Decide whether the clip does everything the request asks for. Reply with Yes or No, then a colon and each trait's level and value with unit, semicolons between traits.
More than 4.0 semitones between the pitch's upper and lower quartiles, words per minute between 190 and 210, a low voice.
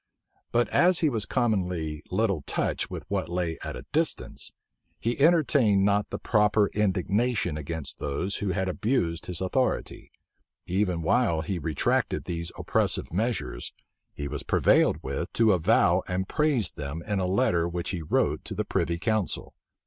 No: average, 4.7 semitones; average, 155 wpm; very low, 95 Hz